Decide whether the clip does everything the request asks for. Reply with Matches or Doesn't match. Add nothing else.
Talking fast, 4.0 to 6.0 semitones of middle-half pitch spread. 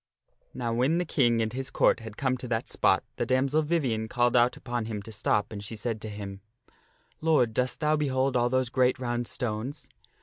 Doesn't match